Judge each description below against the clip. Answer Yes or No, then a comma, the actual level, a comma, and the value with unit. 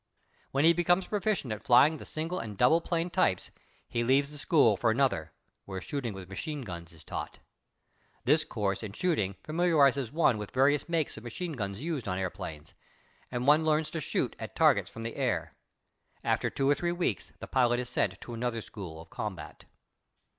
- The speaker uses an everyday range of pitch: No, wide, 6.9 semitones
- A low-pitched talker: Yes, low, 130 Hz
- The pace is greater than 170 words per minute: Yes, average, 190 wpm